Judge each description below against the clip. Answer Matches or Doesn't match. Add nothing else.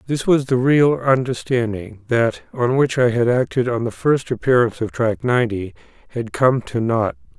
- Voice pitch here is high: Doesn't match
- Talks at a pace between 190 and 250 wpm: Doesn't match